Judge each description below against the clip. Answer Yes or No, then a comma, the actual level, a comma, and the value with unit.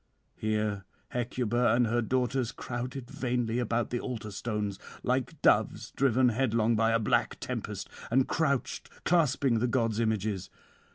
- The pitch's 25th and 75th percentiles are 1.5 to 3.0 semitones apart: Yes, narrow, 2.4 semitones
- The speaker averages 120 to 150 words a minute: Yes, slow, 135 wpm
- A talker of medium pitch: No, low, 120 Hz